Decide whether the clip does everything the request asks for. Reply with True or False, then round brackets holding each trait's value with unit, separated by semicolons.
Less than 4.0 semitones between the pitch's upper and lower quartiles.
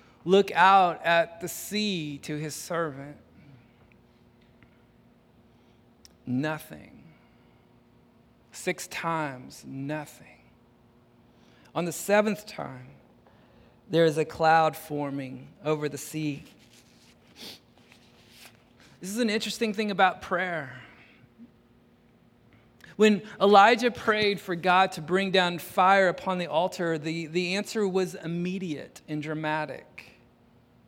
False (4.4 semitones)